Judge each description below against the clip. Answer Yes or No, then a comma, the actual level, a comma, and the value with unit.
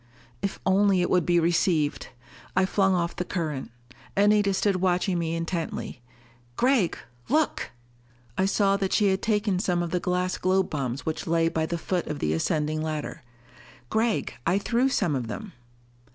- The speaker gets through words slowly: No, average, 170 wpm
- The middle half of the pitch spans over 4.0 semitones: No, average, 3.2 semitones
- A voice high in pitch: No, medium, 180 Hz